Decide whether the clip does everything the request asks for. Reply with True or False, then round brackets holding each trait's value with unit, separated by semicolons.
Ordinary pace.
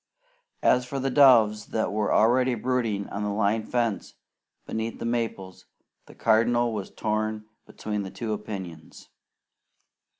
False (130 wpm)